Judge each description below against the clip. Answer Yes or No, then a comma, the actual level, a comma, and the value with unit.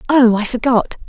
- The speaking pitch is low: No, high, 240 Hz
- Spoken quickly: No, average, 165 wpm